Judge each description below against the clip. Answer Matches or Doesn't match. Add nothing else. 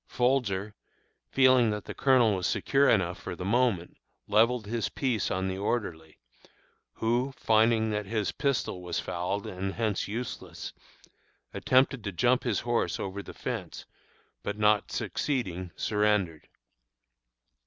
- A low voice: Matches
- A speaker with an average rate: Doesn't match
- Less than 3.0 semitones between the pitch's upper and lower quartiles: Doesn't match